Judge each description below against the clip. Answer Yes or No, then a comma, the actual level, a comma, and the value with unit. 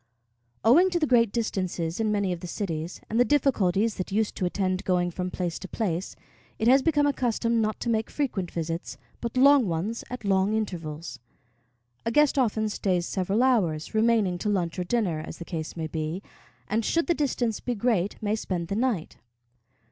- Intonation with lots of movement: No, average, 4.9 semitones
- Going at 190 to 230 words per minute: Yes, average, 195 wpm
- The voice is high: Yes, high, 205 Hz